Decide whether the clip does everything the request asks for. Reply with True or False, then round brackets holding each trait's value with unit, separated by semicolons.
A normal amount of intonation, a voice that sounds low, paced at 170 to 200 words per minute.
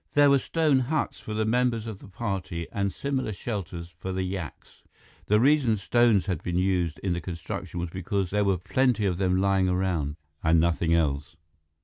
True (4.2 semitones; 95 Hz; 190 wpm)